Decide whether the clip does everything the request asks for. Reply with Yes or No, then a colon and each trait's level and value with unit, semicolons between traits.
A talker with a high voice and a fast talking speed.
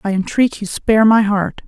Yes: high, 210 Hz; fast, 215 wpm